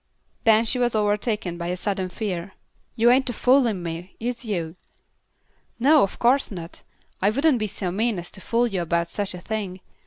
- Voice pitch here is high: Yes, high, 210 Hz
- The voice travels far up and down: No, average, 4.7 semitones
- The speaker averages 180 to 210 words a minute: Yes, average, 190 wpm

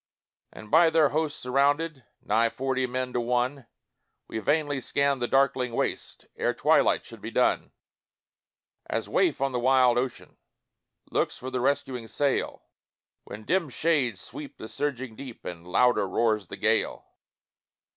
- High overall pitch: No, low, 130 Hz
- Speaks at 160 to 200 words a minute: No, average, 145 wpm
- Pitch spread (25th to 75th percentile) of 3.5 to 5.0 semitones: No, average, 2.9 semitones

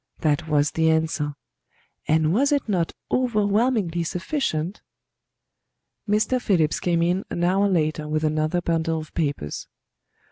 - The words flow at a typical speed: No, slow, 130 wpm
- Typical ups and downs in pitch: Yes, average, 4.5 semitones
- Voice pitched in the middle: Yes, medium, 170 Hz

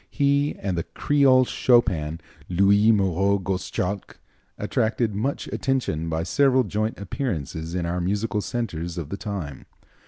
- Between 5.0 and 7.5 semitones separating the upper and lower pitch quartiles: Yes, wide, 5.6 semitones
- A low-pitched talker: Yes, low, 100 Hz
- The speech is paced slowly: Yes, slow, 130 wpm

